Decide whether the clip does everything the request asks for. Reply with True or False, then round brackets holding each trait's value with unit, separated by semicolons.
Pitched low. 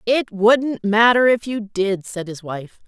False (215 Hz)